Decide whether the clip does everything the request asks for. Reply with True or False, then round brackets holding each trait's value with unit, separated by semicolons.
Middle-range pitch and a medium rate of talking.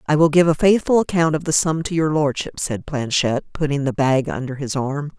False (150 Hz; 230 wpm)